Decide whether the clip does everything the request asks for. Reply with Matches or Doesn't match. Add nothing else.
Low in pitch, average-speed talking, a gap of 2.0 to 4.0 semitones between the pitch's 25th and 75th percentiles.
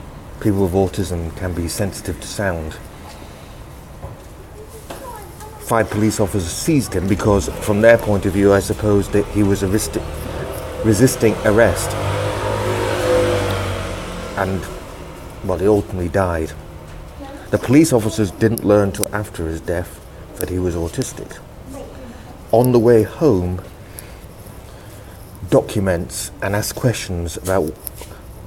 Doesn't match